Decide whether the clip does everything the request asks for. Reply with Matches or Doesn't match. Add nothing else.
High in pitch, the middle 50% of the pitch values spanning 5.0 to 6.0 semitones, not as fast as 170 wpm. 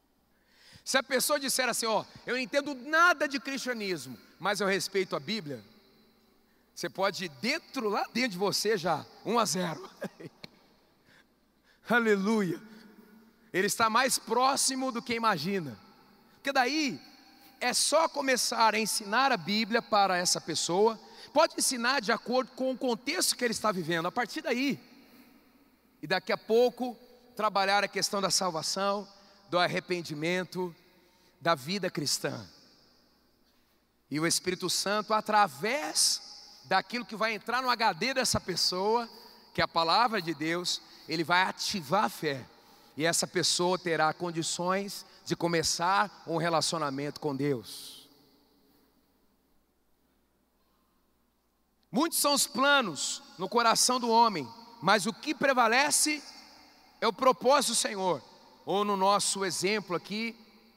Matches